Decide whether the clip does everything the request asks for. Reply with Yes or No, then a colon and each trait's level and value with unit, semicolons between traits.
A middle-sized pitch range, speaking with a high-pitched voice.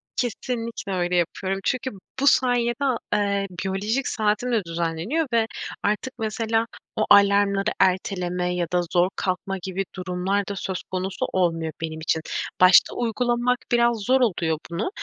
Yes: average, 4.4 semitones; high, 200 Hz